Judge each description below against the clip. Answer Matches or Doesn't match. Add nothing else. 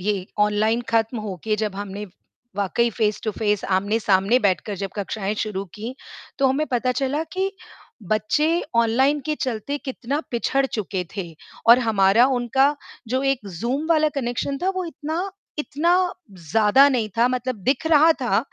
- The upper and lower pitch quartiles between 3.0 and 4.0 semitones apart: Doesn't match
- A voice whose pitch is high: Matches